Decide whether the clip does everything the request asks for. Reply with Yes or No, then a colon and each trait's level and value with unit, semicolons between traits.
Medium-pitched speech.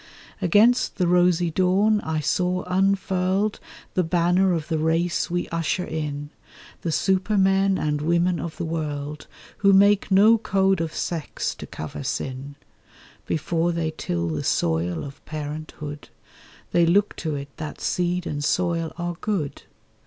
Yes: medium, 170 Hz